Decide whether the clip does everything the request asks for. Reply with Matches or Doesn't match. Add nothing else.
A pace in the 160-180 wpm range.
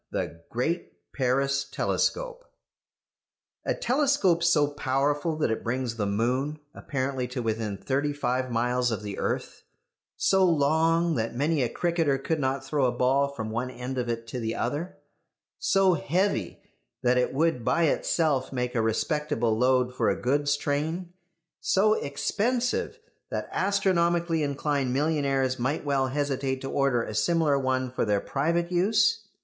Doesn't match